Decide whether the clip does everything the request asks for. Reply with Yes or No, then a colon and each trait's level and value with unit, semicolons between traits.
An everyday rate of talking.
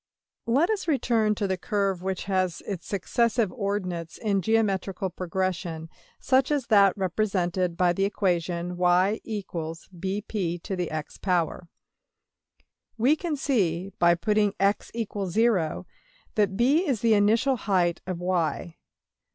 No: slow, 110 wpm